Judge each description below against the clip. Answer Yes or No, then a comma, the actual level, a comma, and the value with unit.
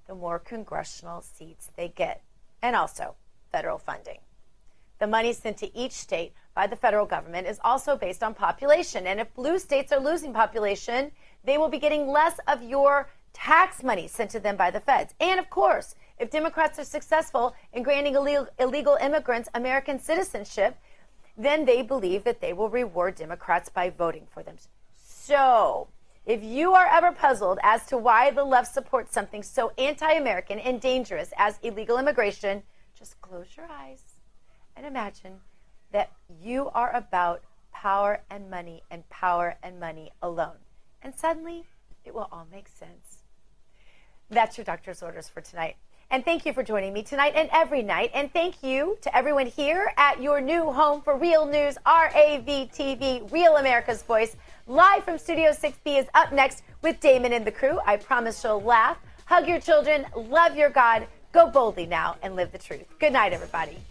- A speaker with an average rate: Yes, average, 170 wpm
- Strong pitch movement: Yes, wide, 6.3 semitones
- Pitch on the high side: Yes, very high, 260 Hz